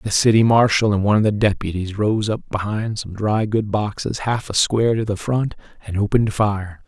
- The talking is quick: Yes, fast, 210 wpm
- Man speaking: Yes, male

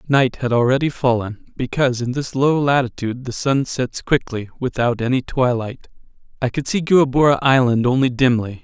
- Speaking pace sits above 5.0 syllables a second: Yes, 5.2 syllables/s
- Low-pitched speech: Yes, low, 130 Hz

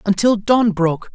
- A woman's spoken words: No, male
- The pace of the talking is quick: No, average, 155 wpm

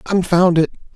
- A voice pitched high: No, medium, 170 Hz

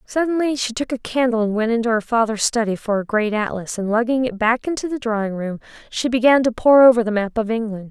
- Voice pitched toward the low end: No, high, 230 Hz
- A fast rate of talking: Yes, fast, 245 wpm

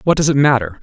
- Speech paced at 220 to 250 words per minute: No, fast, 290 wpm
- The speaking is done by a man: Yes, male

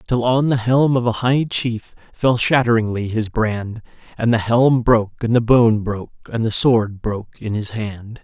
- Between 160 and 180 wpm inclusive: No, average, 195 wpm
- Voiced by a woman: No, male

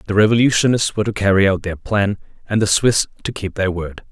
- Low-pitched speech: Yes, low, 100 Hz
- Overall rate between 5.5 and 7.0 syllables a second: Yes, 6.1 syllables/s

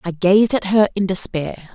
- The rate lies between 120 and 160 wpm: No, fast, 205 wpm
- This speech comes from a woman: Yes, female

